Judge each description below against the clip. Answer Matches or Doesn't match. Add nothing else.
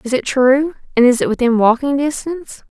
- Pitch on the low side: Doesn't match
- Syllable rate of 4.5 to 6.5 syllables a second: Matches